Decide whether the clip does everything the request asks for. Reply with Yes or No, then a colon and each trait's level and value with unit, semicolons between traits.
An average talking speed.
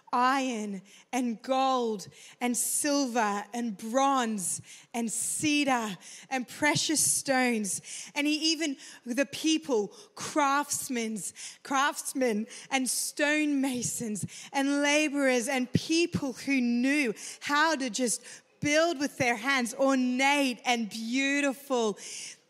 No: slow, 95 wpm